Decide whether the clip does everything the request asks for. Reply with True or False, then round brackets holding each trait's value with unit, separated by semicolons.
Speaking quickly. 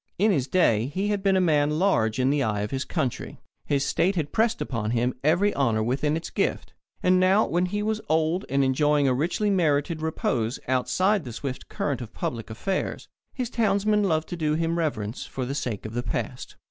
True (210 wpm)